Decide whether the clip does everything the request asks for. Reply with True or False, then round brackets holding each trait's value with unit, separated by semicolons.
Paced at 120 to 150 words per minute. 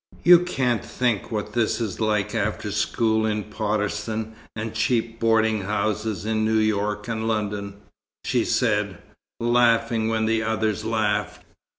True (135 wpm)